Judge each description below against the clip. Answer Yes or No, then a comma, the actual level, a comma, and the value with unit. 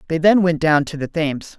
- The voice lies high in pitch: No, medium, 160 Hz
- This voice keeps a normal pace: No, fast, 265 wpm